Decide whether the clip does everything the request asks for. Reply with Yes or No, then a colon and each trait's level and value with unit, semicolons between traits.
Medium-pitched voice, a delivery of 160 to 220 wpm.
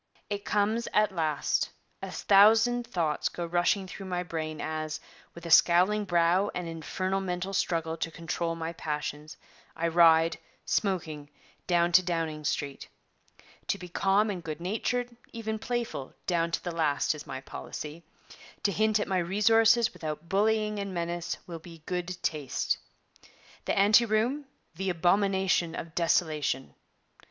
No: medium, 175 Hz; average, 145 wpm